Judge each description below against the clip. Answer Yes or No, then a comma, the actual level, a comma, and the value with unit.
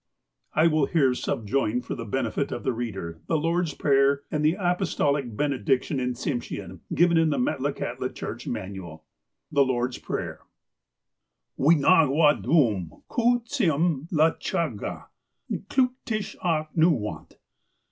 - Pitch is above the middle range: No, medium, 145 Hz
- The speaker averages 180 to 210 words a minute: No, slow, 135 wpm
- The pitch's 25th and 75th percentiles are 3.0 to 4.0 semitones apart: No, average, 5.2 semitones